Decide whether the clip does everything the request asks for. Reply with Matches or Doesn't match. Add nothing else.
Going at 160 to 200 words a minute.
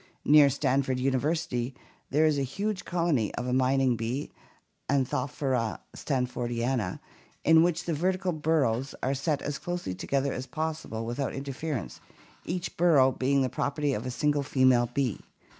Doesn't match